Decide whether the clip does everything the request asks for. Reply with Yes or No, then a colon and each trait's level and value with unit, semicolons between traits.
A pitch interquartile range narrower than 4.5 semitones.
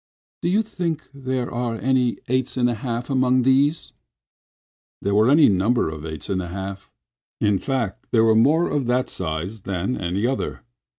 No: average, 5.1 semitones